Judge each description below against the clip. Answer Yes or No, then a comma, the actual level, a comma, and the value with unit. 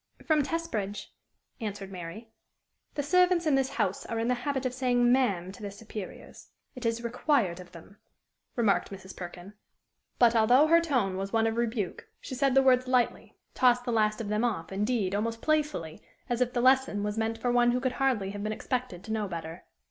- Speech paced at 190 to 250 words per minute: Yes, average, 200 wpm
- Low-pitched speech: No, high, 230 Hz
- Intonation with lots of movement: No, average, 4.0 semitones